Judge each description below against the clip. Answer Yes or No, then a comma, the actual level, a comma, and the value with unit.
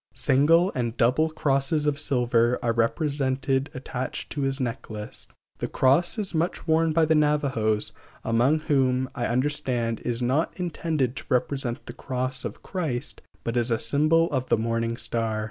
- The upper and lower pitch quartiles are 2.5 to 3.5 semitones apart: No, average, 4.0 semitones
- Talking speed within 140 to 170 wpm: Yes, average, 165 wpm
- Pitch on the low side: Yes, low, 130 Hz